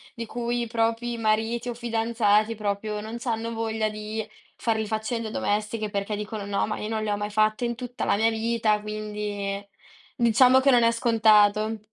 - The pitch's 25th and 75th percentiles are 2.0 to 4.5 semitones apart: No, narrow, 1.6 semitones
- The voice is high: Yes, high, 220 Hz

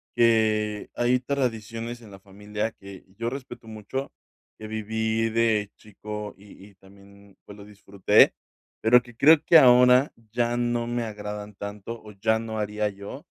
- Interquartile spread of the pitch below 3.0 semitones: Yes, narrow, 2.5 semitones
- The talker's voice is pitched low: Yes, low, 110 Hz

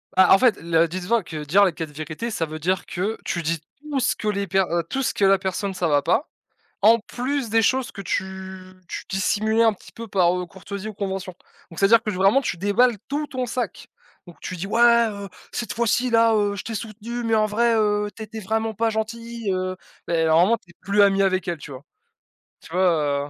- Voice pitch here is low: No, high, 200 Hz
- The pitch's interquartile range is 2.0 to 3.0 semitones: No, average, 3.8 semitones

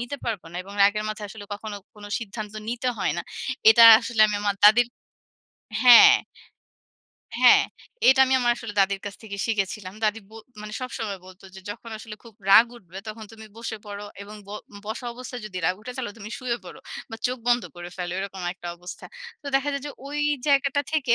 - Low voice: No, high, 220 Hz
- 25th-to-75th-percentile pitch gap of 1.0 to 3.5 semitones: Yes, average, 3.2 semitones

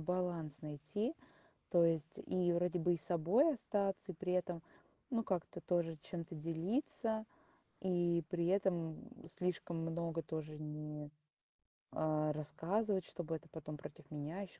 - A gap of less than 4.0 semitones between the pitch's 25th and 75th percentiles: Yes, average, 2.7 semitones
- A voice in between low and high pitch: Yes, medium, 170 Hz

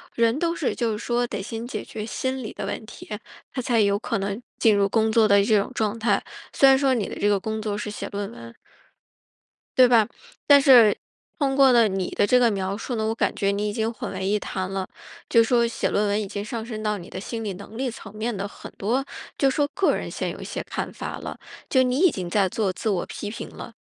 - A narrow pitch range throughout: No, average, 3.1 semitones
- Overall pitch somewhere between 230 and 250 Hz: No, high, 220 Hz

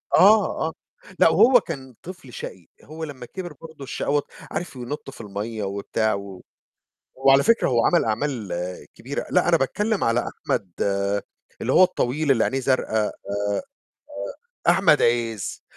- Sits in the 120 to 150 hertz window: Yes, low, 135 Hz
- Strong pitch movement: Yes, wide, 6.0 semitones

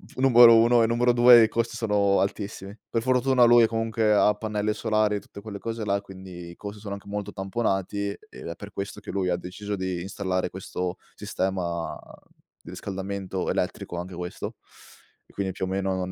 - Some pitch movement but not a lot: Yes, average, 3.0 semitones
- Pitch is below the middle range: Yes, low, 100 Hz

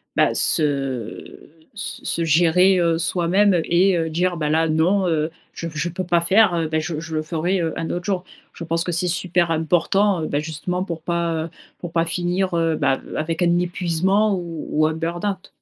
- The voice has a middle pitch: Yes, medium, 170 Hz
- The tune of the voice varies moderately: No, narrow, 2.0 semitones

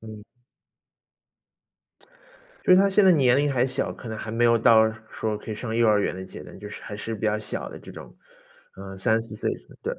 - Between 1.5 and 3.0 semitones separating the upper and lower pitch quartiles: Yes, average, 2.7 semitones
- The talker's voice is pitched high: No, low, 110 Hz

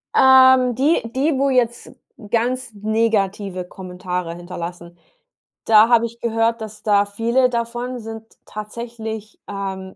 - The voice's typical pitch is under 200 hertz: No, high, 225 Hz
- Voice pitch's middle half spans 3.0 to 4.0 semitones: Yes, average, 3.4 semitones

